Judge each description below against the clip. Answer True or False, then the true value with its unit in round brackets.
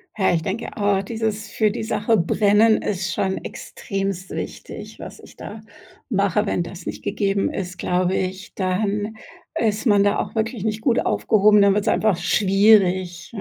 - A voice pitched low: False (200 Hz)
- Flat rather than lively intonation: True (2.3 semitones)